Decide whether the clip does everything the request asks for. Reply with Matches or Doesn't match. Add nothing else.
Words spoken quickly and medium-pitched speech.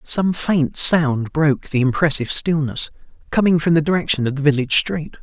Doesn't match